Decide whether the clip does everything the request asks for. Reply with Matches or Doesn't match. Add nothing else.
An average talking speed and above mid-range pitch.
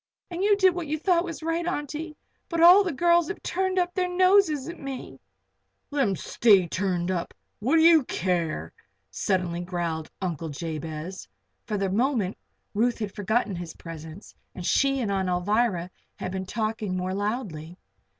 Matches